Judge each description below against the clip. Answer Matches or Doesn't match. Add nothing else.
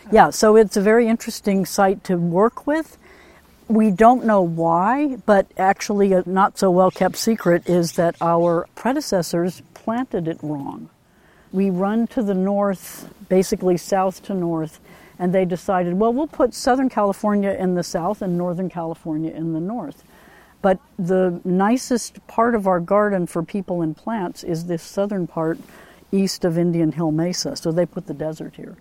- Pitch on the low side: Doesn't match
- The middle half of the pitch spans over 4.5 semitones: Doesn't match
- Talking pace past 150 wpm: Matches